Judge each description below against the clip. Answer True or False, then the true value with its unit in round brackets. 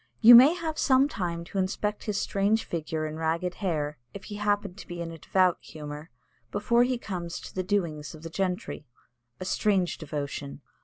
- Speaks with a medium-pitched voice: True (180 Hz)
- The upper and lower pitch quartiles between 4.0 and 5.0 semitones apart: True (4.4 semitones)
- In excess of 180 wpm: True (190 wpm)